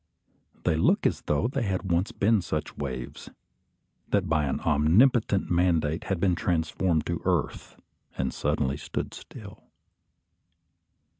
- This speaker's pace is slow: Yes, slow, 130 wpm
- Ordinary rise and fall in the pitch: Yes, average, 4.2 semitones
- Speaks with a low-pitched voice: Yes, very low, 85 Hz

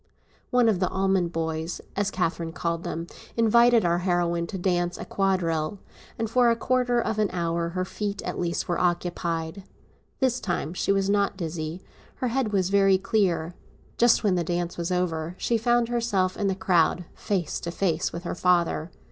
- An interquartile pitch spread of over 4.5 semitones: No, average, 3.3 semitones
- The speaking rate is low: No, average, 180 wpm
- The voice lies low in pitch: No, medium, 185 Hz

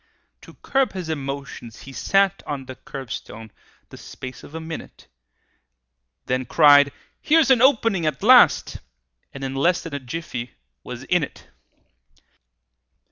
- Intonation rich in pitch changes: Yes, wide, 6.2 semitones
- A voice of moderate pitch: Yes, medium, 145 Hz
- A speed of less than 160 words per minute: Yes, slow, 135 wpm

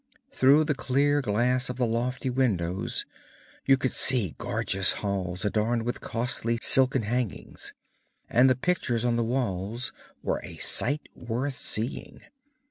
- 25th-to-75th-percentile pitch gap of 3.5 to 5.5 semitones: No, average, 2.9 semitones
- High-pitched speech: No, low, 120 Hz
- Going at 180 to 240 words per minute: No, slow, 135 wpm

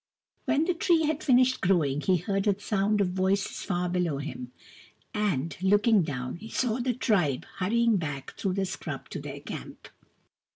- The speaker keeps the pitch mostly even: No, average, 4.6 semitones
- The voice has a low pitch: No, high, 195 Hz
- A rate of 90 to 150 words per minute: No, average, 170 wpm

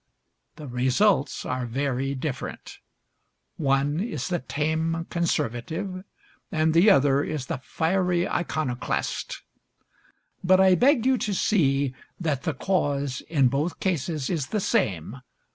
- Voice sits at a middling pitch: Yes, medium, 155 Hz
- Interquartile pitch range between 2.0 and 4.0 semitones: No, average, 5.0 semitones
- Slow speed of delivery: Yes, slow, 125 wpm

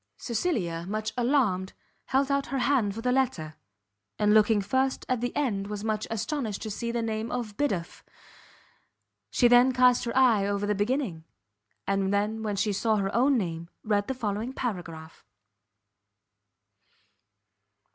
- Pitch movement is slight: No, average, 3.9 semitones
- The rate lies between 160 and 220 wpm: No, average, 145 wpm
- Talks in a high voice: Yes, high, 220 Hz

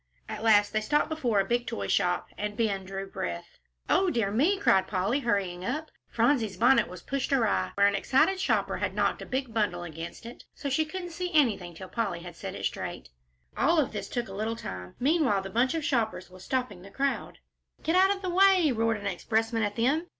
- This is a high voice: Yes, high, 225 Hz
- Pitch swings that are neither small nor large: No, wide, 6.4 semitones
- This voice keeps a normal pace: No, fast, 215 wpm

